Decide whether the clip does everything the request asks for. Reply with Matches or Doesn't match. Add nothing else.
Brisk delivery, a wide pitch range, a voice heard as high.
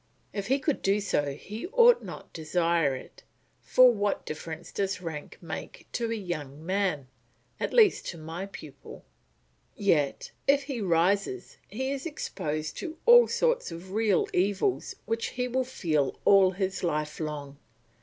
Doesn't match